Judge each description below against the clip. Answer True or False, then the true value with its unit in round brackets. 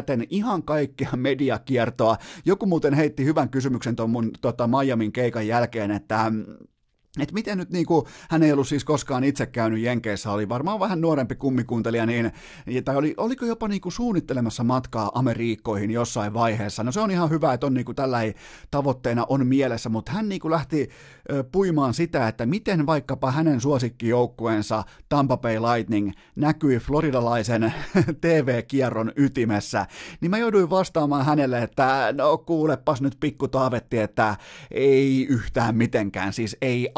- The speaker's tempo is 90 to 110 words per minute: False (150 wpm)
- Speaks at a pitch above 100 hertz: True (130 Hz)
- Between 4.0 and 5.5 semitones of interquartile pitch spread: True (4.6 semitones)